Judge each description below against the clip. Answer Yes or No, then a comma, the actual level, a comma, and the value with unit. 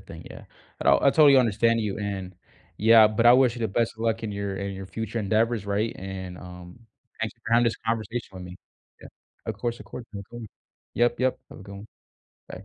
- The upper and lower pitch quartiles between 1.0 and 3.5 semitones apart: Yes, average, 2.9 semitones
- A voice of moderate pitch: No, low, 110 Hz